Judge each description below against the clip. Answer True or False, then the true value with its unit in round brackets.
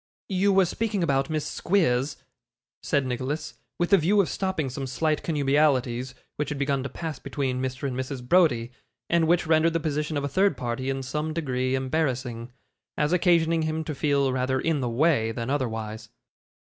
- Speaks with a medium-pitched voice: True (145 Hz)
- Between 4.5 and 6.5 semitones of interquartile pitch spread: False (4.0 semitones)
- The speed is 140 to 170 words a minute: False (180 wpm)